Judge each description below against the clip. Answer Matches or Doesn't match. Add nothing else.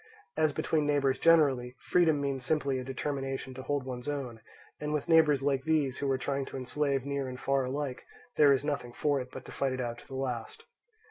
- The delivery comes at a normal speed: Doesn't match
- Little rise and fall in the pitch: Matches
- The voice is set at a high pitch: Doesn't match